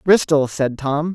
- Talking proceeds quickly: No, average, 160 wpm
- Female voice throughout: No, male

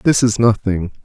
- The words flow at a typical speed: Yes, average, 175 wpm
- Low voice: Yes, low, 110 Hz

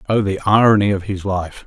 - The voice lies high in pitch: No, low, 100 Hz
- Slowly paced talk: No, fast, 215 wpm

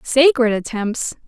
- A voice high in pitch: Yes, very high, 250 Hz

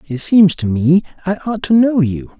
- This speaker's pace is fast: Yes, fast, 225 wpm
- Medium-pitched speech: Yes, medium, 175 Hz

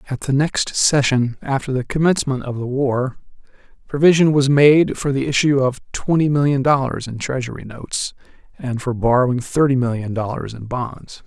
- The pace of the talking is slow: No, average, 165 wpm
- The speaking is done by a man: Yes, male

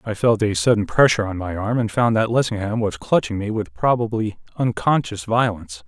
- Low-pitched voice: Yes, low, 105 Hz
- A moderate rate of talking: Yes, average, 195 wpm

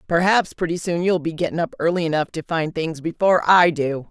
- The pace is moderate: No, fast, 220 wpm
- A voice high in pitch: No, medium, 165 Hz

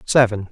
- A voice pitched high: No, low, 110 Hz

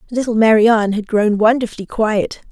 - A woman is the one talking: Yes, female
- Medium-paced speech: Yes, average, 145 wpm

